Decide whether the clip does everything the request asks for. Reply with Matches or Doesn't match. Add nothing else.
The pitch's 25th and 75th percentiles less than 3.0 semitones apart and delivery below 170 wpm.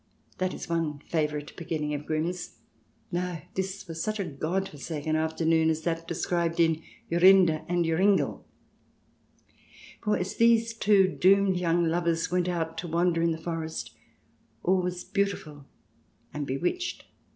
Matches